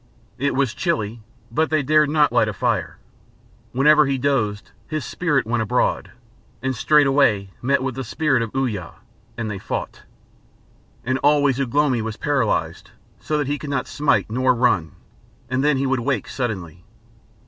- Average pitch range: Yes, average, 4.2 semitones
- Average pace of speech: Yes, average, 165 wpm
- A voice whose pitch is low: Yes, low, 130 Hz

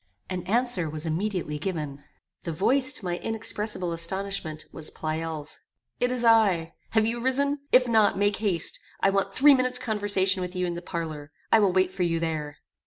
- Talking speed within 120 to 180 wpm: No, average, 190 wpm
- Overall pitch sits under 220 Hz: Yes, high, 190 Hz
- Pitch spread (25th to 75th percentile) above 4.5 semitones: Yes, average, 5.2 semitones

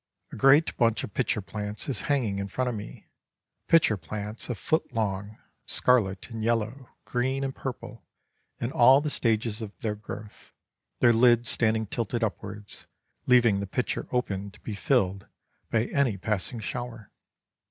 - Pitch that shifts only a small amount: No, average, 3.2 semitones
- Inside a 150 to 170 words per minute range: Yes, average, 155 wpm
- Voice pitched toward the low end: Yes, low, 115 Hz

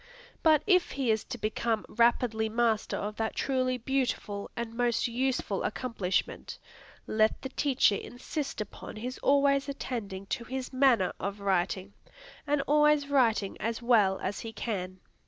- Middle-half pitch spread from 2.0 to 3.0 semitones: No, average, 4.0 semitones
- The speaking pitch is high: Yes, high, 235 Hz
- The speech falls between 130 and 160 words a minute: Yes, average, 145 wpm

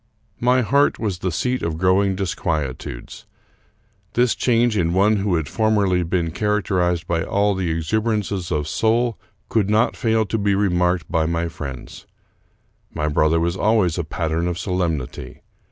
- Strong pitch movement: No, average, 4.4 semitones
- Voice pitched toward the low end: Yes, very low, 95 Hz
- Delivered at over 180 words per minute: No, average, 155 wpm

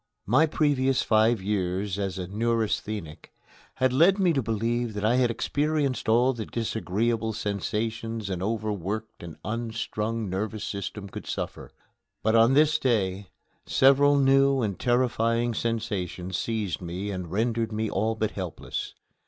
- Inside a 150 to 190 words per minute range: No, average, 140 wpm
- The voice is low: Yes, low, 110 Hz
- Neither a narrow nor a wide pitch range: Yes, average, 3.1 semitones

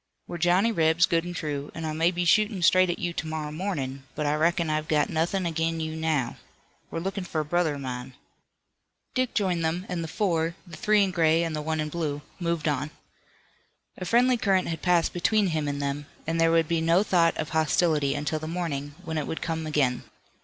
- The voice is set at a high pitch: No, medium, 165 Hz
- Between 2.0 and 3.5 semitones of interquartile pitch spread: Yes, narrow, 2.4 semitones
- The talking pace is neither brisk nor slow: No, fast, 220 wpm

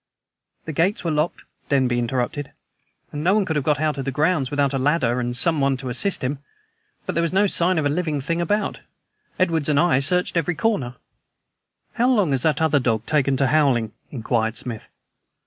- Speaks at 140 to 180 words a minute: No, average, 200 wpm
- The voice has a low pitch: No, medium, 145 Hz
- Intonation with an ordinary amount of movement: Yes, average, 4.4 semitones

